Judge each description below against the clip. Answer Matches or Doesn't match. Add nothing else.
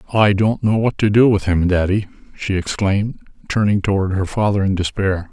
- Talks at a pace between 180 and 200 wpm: Matches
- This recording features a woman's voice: Doesn't match